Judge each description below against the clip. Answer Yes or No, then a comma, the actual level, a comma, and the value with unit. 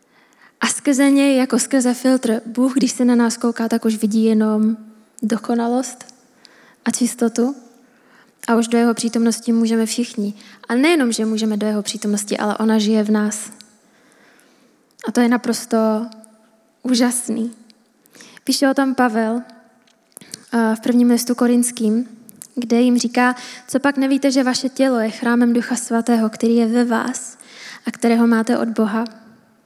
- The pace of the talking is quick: No, average, 150 wpm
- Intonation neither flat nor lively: No, narrow, 1.8 semitones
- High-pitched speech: Yes, high, 235 Hz